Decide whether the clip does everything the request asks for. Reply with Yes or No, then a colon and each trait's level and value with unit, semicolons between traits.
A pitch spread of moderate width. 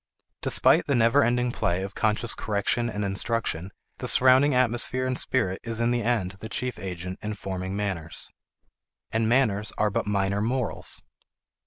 Yes: average, 3.7 semitones